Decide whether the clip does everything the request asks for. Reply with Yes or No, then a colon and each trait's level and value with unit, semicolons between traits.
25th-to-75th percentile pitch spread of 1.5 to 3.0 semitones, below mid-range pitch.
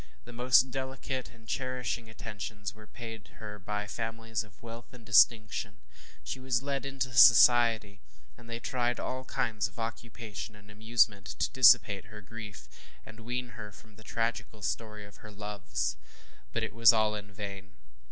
Yes: narrow, 2.4 semitones; low, 110 Hz